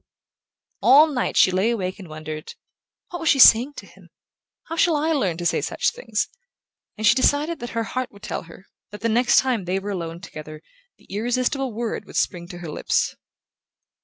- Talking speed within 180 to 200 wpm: Yes, average, 195 wpm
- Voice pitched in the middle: No, high, 220 Hz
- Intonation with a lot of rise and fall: Yes, wide, 6.5 semitones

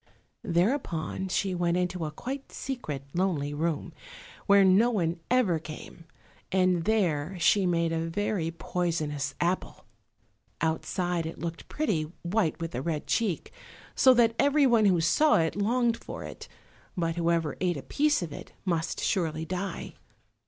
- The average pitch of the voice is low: No, medium, 175 Hz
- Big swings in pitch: No, average, 3.9 semitones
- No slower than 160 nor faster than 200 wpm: No, average, 145 wpm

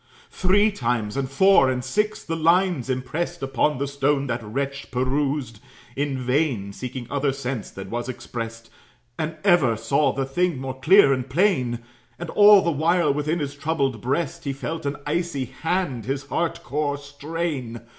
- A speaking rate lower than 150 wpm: No, average, 165 wpm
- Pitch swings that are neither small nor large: Yes, average, 4.2 semitones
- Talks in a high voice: No, medium, 140 Hz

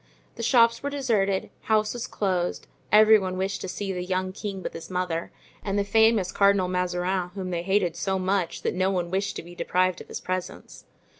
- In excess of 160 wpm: Yes, average, 200 wpm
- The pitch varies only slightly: Yes, narrow, 2.1 semitones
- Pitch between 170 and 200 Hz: Yes, high, 190 Hz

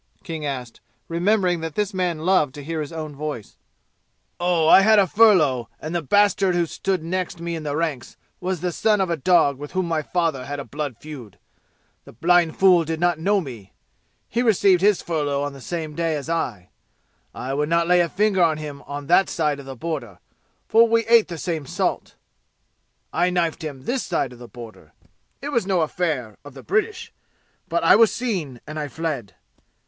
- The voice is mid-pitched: Yes, medium, 165 Hz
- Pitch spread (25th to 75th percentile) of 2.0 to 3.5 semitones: No, average, 4.2 semitones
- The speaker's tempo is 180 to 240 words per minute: Yes, average, 195 wpm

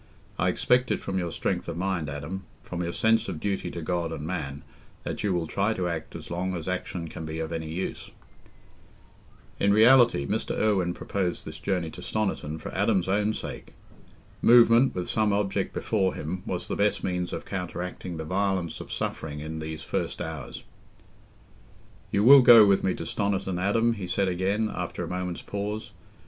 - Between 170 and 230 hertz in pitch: No, very low, 95 Hz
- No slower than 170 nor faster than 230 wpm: Yes, average, 180 wpm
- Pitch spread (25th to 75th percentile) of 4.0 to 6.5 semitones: No, average, 3.3 semitones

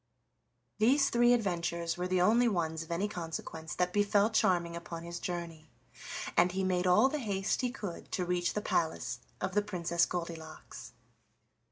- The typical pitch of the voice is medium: Yes, medium, 180 Hz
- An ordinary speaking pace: Yes, average, 165 wpm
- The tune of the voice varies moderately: Yes, average, 3.4 semitones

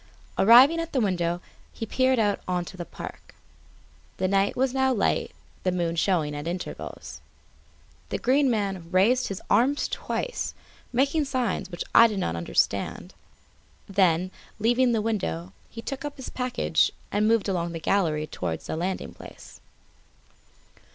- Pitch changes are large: Yes, wide, 6.4 semitones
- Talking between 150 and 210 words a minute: Yes, average, 155 wpm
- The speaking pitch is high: Yes, high, 200 Hz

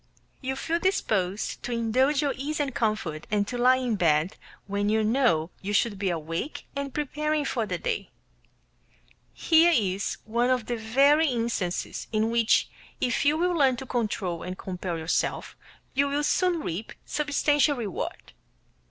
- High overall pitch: Yes, high, 240 Hz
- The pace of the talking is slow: No, average, 160 wpm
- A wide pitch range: Yes, wide, 6.0 semitones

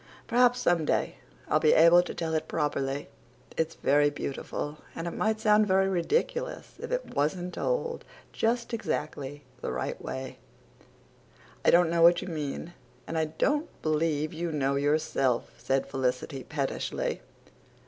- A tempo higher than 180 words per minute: No, average, 150 wpm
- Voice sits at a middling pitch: Yes, medium, 160 Hz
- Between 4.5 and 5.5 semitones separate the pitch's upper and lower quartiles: Yes, average, 4.8 semitones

